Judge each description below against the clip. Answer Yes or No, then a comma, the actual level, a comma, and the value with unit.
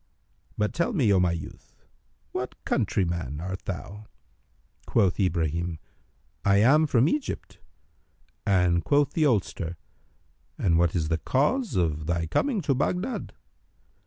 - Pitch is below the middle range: Yes, very low, 95 Hz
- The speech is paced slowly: Yes, slow, 130 wpm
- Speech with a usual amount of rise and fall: No, wide, 8.6 semitones